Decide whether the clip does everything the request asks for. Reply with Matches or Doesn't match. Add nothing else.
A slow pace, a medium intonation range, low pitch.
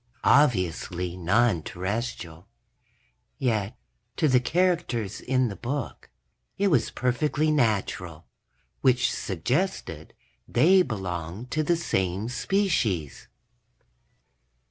Doesn't match